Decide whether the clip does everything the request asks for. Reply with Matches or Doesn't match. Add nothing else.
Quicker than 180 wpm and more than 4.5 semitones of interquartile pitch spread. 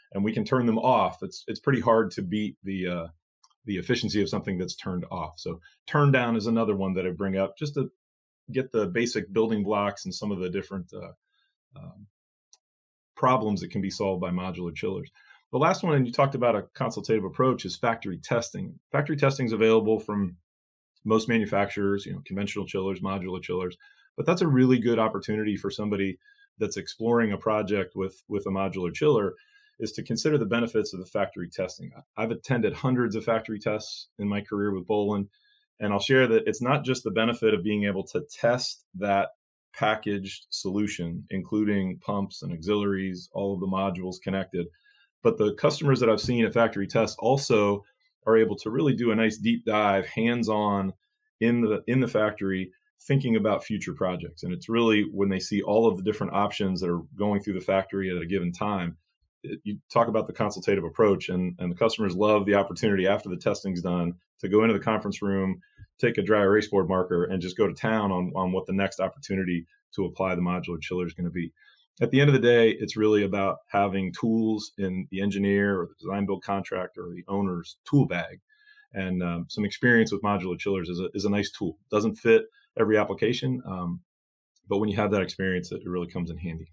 Doesn't match